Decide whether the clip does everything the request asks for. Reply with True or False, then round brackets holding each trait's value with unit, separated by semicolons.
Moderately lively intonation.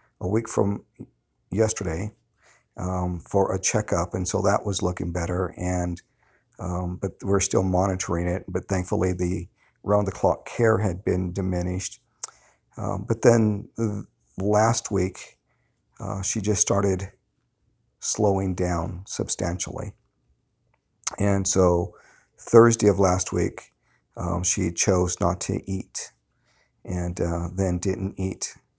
False (2.3 semitones)